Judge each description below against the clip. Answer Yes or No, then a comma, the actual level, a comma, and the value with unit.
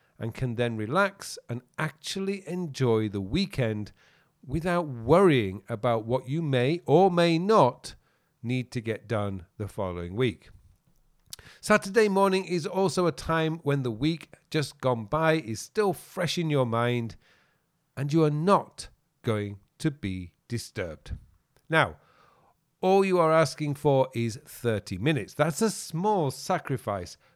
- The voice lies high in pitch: No, medium, 140 Hz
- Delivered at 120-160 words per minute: Yes, average, 140 wpm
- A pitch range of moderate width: No, wide, 6.7 semitones